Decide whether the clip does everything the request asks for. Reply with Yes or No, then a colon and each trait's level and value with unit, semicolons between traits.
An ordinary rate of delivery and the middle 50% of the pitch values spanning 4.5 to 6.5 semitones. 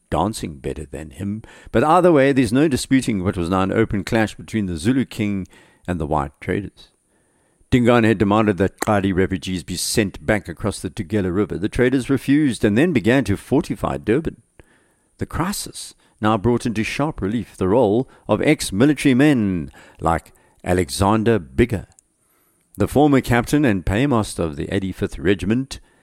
Yes: average, 165 wpm; average, 4.9 semitones